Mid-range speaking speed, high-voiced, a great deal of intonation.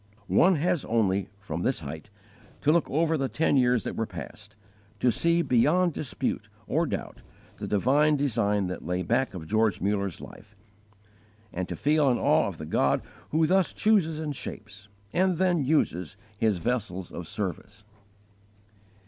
No: average, 160 wpm; low, 120 Hz; wide, 7.8 semitones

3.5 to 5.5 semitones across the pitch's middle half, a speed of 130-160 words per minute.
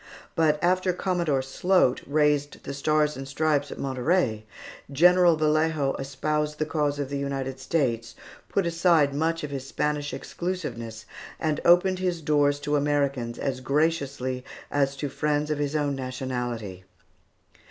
No: average, 2.8 semitones; average, 140 wpm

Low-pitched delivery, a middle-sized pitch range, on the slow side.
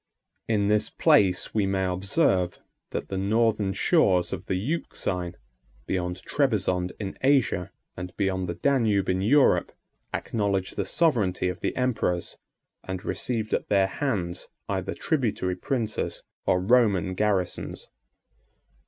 Yes: very low, 95 Hz; average, 3.7 semitones; slow, 125 wpm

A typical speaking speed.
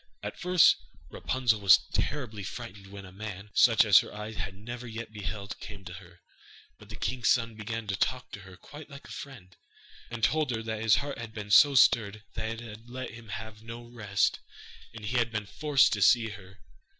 No: fast, 210 wpm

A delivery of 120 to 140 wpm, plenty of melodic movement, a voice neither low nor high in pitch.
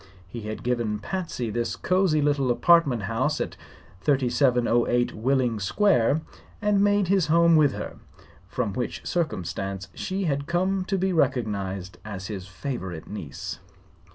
No: slow, 135 wpm; wide, 7.9 semitones; low, 125 Hz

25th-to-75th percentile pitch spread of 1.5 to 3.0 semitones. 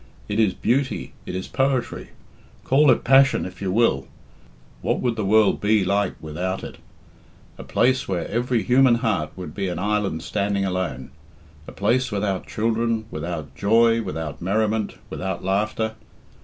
No: average, 3.9 semitones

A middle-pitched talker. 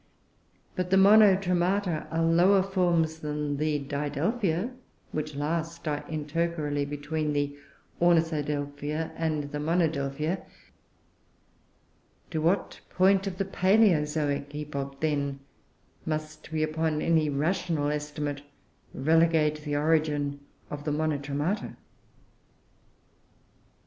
Yes: medium, 155 Hz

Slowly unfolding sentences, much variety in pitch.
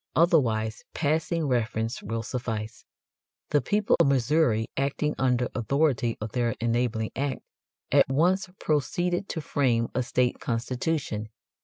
No: slow, 125 wpm; average, 4.8 semitones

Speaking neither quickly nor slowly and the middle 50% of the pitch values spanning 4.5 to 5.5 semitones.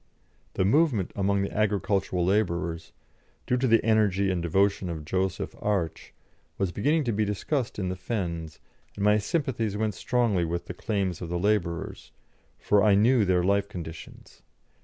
No: average, 160 wpm; average, 3.2 semitones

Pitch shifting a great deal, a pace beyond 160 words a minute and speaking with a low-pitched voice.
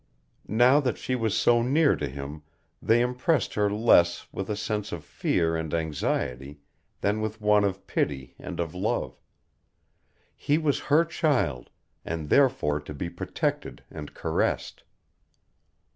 No: wide, 7.9 semitones; average, 145 wpm; low, 105 Hz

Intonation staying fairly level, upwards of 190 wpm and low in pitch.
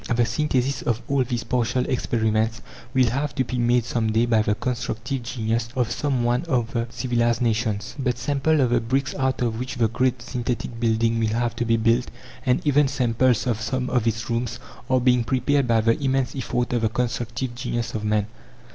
Yes: narrow, 2.0 semitones; average, 200 wpm; low, 120 Hz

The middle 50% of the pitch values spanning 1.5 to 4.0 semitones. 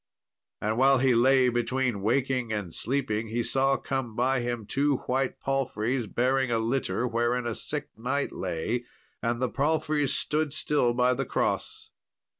Yes: narrow, 2.5 semitones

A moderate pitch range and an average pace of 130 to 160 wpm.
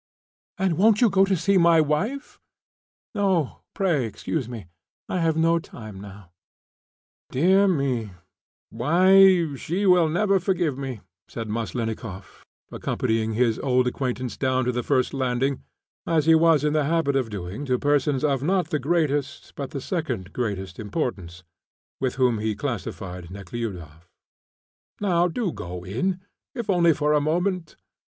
No: wide, 7.0 semitones; average, 150 wpm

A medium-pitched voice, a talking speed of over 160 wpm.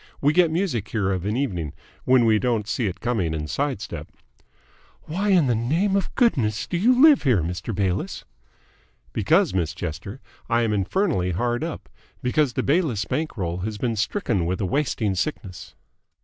No: low, 115 Hz; average, 175 wpm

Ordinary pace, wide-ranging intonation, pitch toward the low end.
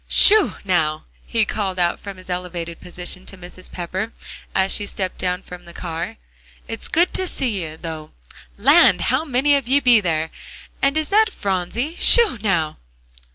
No: average, 170 wpm; wide, 6.8 semitones; high, 190 Hz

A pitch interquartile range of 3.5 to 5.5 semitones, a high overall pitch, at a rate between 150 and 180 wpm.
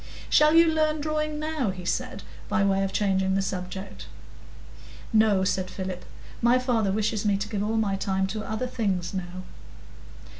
Yes: average, 4.4 semitones; high, 205 Hz; average, 165 wpm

